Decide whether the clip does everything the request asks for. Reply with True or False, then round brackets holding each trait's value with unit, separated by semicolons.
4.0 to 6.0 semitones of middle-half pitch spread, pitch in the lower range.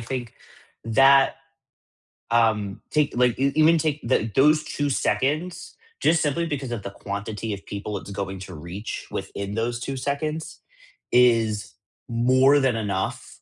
True (5.3 semitones; 120 Hz)